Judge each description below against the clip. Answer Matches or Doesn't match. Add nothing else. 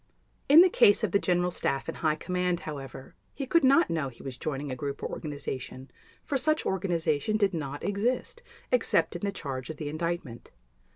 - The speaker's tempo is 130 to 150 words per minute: Doesn't match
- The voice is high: Doesn't match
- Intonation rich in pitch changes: Matches